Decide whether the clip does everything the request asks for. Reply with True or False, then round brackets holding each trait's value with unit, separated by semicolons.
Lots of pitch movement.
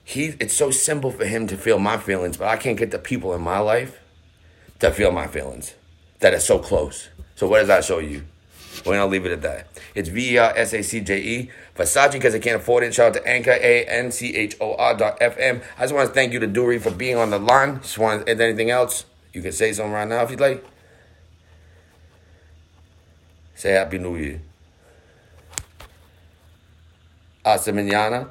True (6.0 semitones)